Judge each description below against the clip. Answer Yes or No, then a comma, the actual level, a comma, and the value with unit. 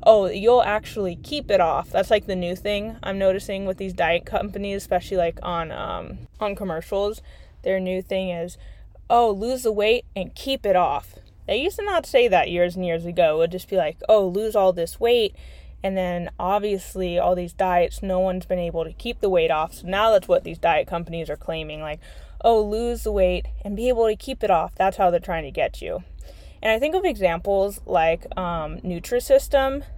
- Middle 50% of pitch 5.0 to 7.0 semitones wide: No, average, 4.0 semitones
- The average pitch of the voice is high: Yes, high, 195 Hz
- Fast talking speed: Yes, fast, 210 wpm